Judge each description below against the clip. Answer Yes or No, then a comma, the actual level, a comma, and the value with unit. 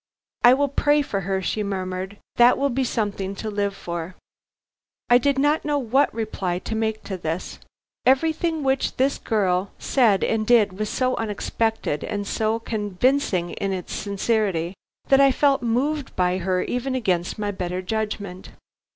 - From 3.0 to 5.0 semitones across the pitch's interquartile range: No, wide, 5.4 semitones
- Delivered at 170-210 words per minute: No, average, 160 wpm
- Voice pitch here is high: Yes, high, 215 Hz